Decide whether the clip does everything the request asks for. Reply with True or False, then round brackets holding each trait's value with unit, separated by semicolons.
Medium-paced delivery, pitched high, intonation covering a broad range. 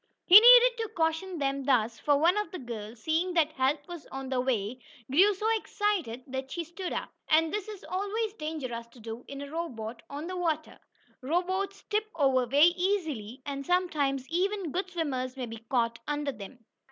True (190 wpm; 300 Hz; 6.1 semitones)